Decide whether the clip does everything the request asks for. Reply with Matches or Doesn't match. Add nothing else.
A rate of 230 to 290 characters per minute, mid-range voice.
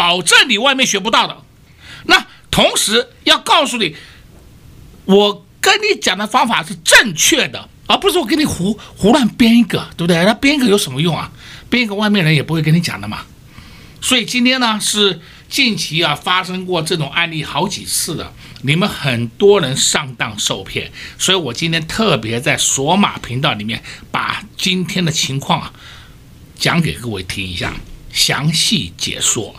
Matches